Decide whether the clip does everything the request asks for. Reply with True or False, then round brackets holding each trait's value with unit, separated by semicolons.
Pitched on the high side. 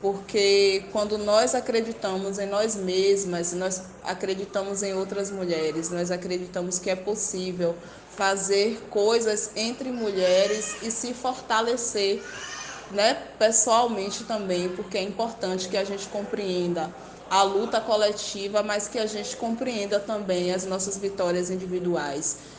True (200 Hz)